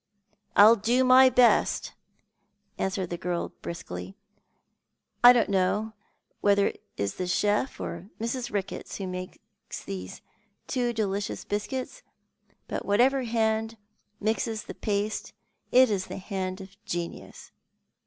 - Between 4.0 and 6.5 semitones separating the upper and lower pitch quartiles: No, average, 3.6 semitones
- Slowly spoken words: Yes, slow, 130 wpm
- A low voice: No, high, 205 Hz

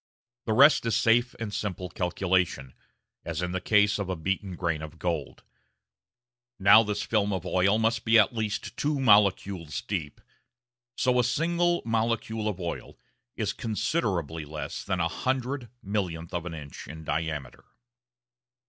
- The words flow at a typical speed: Yes, average, 155 wpm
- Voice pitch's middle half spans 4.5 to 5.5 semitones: Yes, average, 5.1 semitones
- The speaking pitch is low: Yes, low, 100 Hz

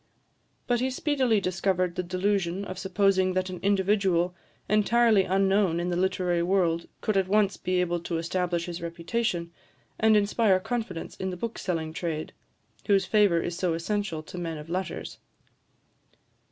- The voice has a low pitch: No, medium, 185 Hz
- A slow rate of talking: No, average, 155 wpm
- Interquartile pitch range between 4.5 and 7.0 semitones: No, average, 2.8 semitones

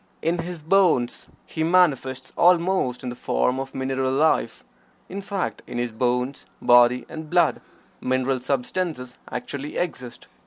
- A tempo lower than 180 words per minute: Yes, average, 140 wpm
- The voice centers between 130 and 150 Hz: Yes, low, 135 Hz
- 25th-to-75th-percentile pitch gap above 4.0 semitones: Yes, average, 5.2 semitones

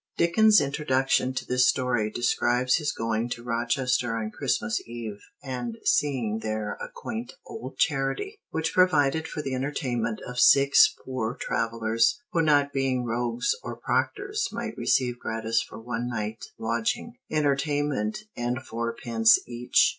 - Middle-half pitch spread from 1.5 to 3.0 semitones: No, average, 3.5 semitones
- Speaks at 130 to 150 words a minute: Yes, average, 140 wpm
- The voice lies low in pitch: Yes, low, 125 Hz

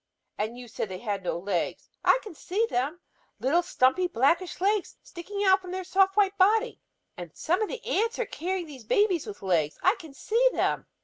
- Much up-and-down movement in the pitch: Yes, wide, 8.4 semitones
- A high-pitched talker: Yes, very high, 355 Hz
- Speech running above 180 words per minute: Yes, average, 200 wpm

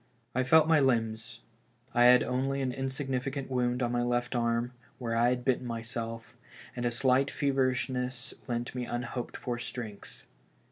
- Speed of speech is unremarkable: Yes, average, 155 wpm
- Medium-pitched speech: No, low, 125 Hz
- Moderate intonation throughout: No, narrow, 1.6 semitones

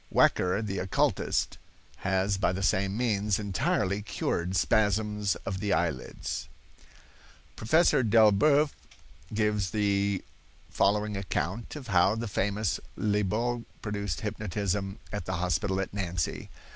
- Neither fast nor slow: No, slow, 120 wpm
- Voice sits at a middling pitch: No, low, 100 Hz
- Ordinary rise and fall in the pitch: No, narrow, 2.1 semitones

